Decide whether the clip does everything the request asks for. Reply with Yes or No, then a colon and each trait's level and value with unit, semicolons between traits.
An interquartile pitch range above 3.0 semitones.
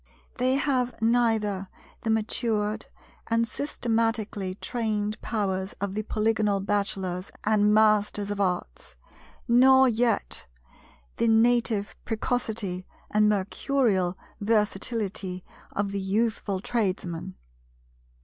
No: narrow, 2.6 semitones